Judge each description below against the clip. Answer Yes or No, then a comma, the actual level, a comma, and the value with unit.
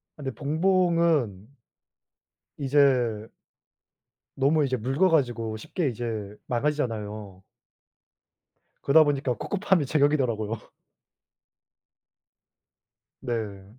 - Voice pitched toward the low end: Yes, low, 130 Hz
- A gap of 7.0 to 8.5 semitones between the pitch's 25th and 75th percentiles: No, average, 5.3 semitones